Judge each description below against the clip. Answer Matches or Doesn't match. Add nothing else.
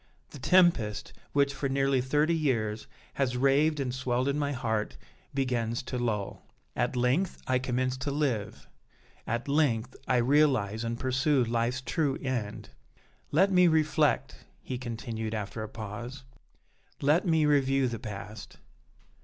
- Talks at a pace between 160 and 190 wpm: Doesn't match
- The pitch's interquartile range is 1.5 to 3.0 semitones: Doesn't match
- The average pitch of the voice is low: Matches